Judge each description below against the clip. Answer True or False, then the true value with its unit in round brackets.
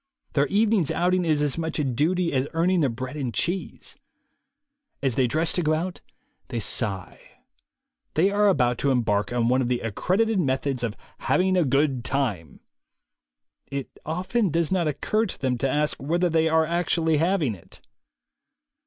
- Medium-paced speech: True (170 wpm)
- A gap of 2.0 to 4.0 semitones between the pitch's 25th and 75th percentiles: False (5.4 semitones)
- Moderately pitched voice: True (150 Hz)